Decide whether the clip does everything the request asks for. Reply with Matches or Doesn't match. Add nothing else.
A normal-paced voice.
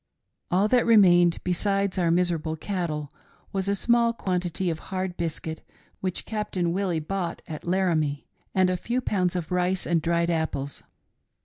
Matches